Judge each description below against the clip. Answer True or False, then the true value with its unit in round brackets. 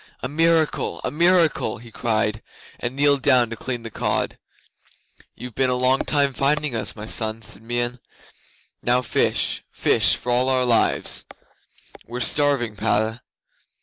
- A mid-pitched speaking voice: False (125 Hz)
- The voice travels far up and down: False (3.6 semitones)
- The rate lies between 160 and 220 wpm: False (150 wpm)